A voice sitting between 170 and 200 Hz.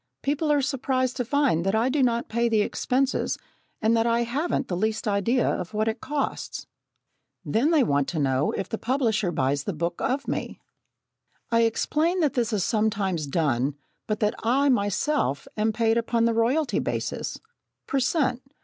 No: high, 230 Hz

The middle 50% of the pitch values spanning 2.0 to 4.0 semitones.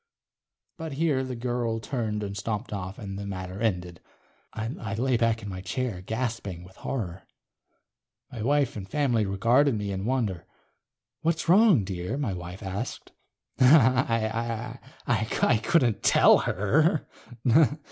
No: average, 4.7 semitones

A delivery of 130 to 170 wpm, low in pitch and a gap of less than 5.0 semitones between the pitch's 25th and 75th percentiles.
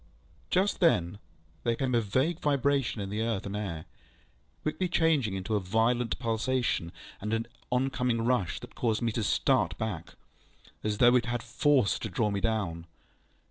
Yes: average, 165 wpm; low, 115 Hz; average, 3.7 semitones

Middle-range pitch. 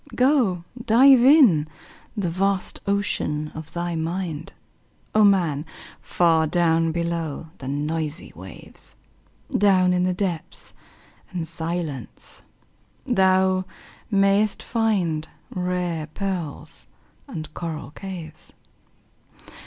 Yes: medium, 175 Hz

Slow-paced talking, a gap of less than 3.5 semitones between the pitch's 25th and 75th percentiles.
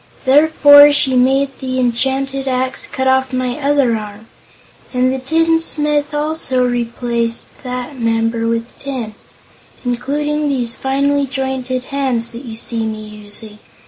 Yes: slow, 130 wpm; average, 2.9 semitones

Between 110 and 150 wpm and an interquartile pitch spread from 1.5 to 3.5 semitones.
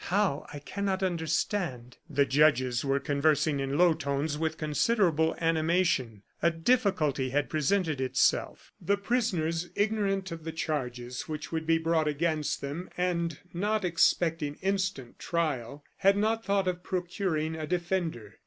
No: average, 140 wpm; average, 4.3 semitones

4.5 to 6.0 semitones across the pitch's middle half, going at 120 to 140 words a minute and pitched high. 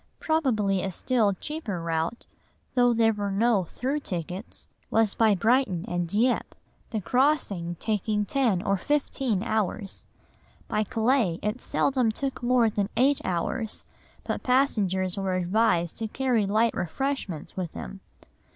Yes: average, 4.9 semitones; slow, 135 wpm; high, 215 Hz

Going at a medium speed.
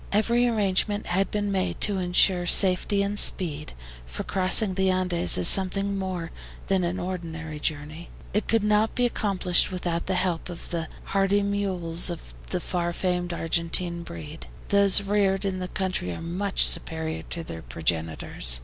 Yes: average, 160 wpm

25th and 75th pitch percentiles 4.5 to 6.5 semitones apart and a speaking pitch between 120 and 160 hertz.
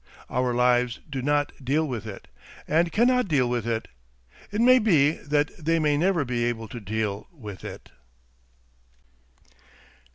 Yes: average, 5.2 semitones; medium, 140 Hz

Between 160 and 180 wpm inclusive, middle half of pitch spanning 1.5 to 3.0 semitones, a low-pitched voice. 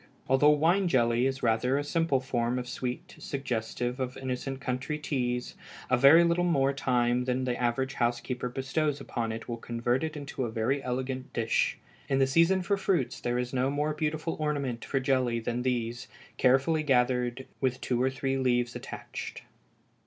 Yes: average, 175 wpm; narrow, 2.4 semitones; low, 130 Hz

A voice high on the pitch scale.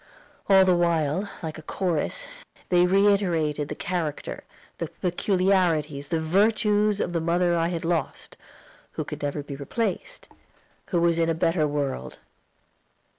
No: medium, 170 Hz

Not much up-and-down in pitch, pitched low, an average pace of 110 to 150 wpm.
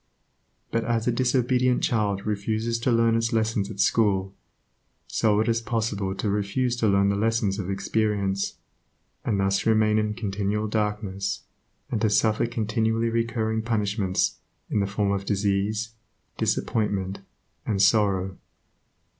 Yes: narrow, 2.3 semitones; low, 105 Hz; average, 140 wpm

